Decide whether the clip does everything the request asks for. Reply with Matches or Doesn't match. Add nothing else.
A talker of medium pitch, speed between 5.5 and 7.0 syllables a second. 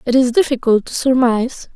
Doesn't match